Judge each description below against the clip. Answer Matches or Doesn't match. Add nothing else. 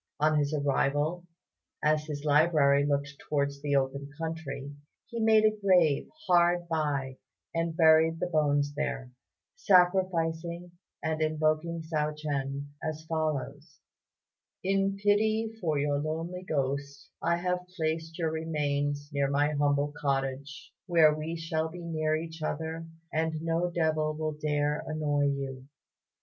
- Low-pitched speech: Doesn't match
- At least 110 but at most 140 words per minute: Matches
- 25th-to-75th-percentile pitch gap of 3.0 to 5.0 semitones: Doesn't match